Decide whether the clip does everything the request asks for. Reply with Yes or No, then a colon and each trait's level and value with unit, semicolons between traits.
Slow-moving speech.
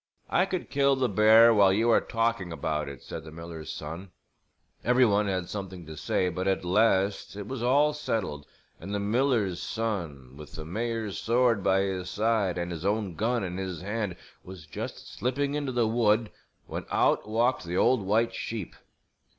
No: average, 185 wpm